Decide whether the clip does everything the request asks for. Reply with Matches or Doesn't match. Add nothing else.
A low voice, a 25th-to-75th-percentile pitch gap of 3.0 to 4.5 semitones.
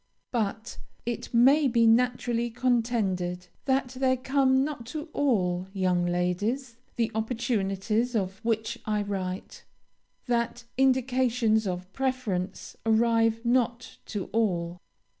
Doesn't match